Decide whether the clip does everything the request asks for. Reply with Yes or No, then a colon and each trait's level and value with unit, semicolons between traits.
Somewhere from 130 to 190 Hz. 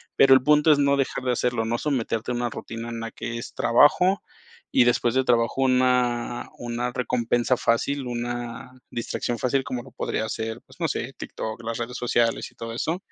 No: low, 120 Hz